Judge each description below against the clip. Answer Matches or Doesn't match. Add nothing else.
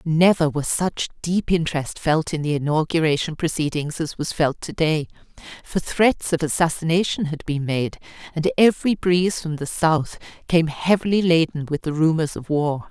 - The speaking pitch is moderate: Matches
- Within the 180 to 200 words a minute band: Doesn't match